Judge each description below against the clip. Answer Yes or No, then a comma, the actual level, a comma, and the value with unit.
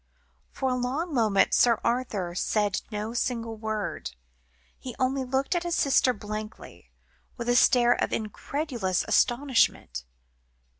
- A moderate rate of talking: No, slow, 130 wpm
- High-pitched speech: Yes, high, 240 Hz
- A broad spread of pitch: No, average, 3.5 semitones